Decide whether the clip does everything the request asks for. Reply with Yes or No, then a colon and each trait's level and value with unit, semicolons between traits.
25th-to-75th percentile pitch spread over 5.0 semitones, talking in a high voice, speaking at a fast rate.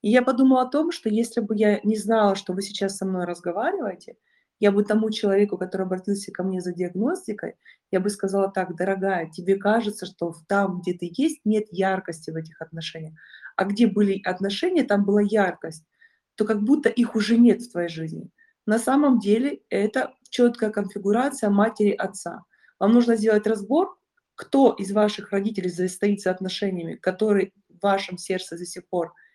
No: average, 3.2 semitones; high, 205 Hz; fast, 175 wpm